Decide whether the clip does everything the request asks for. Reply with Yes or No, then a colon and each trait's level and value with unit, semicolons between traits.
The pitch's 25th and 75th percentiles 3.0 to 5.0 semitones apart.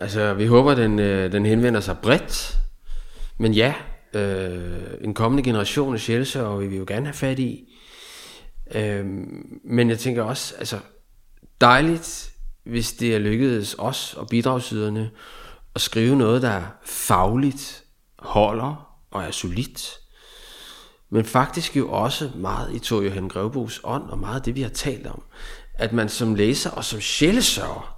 Yes: average, 3.7 semitones